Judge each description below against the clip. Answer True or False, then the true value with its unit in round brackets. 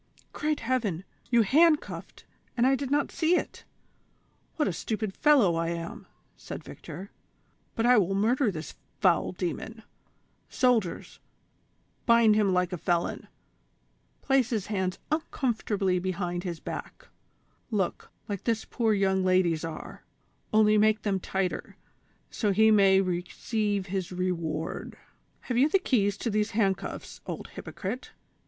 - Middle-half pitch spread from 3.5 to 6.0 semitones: True (4.2 semitones)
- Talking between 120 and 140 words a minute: True (135 wpm)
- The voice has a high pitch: True (205 Hz)